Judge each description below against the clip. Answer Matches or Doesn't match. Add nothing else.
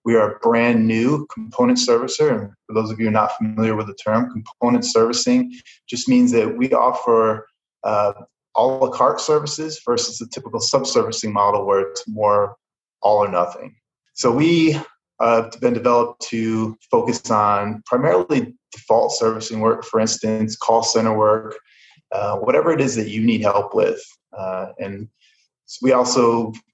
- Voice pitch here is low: Matches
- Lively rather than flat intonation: Doesn't match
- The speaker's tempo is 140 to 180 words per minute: Matches